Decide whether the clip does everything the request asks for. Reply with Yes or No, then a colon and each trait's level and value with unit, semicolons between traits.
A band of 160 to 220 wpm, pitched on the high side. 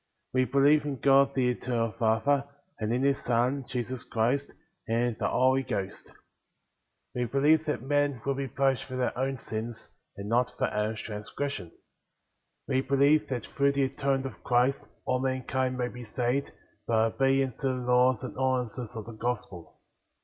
No: average, 180 wpm; low, 130 Hz